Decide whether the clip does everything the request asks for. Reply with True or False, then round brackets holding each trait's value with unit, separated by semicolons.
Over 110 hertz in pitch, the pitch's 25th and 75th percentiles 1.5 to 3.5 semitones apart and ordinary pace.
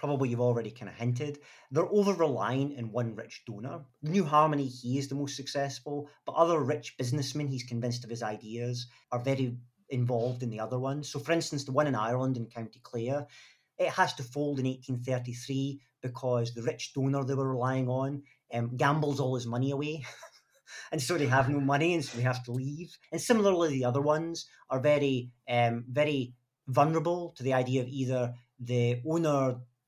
True (135 Hz; 3.0 semitones; 190 wpm)